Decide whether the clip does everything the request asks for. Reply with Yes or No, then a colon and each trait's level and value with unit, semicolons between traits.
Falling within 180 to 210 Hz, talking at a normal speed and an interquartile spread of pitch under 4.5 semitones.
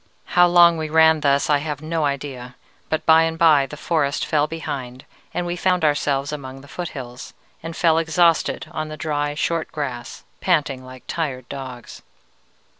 No: medium, 150 Hz; average, 170 wpm; average, 2.9 semitones